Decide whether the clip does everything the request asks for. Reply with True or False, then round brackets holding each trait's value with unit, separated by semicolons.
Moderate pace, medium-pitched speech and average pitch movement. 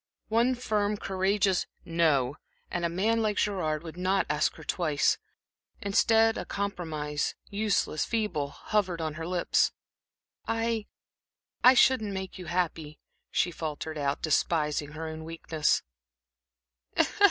False (120 wpm; 175 Hz; 4.8 semitones)